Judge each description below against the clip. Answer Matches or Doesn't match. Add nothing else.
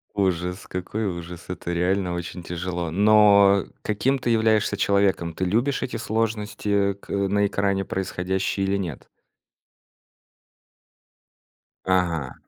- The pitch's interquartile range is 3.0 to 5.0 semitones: Doesn't match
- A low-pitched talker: Matches